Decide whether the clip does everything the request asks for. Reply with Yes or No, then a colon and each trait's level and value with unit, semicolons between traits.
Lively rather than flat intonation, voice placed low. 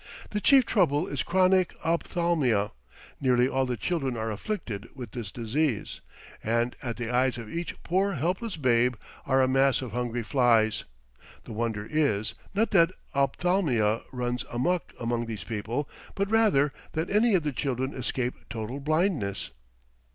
Yes: wide, 6.3 semitones; low, 130 Hz